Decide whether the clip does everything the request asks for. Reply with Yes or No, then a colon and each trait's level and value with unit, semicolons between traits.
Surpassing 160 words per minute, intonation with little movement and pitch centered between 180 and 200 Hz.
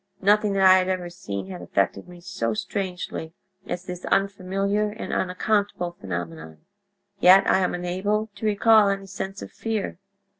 No: average, 155 wpm; narrow, 2.3 semitones; high, 190 Hz